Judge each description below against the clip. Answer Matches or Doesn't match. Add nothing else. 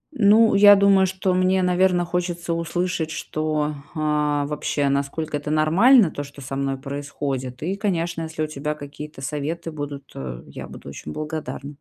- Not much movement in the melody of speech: Doesn't match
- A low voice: Doesn't match